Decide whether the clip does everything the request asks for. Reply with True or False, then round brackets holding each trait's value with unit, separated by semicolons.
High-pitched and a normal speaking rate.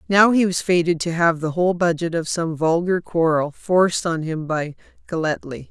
False (170 Hz; 190 wpm)